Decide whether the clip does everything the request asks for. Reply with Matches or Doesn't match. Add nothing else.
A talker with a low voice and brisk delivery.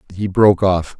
Doesn't match